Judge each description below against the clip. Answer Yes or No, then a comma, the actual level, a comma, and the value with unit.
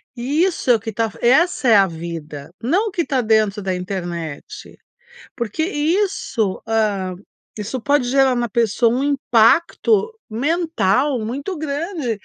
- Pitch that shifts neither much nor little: No, wide, 6.2 semitones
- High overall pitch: Yes, high, 240 Hz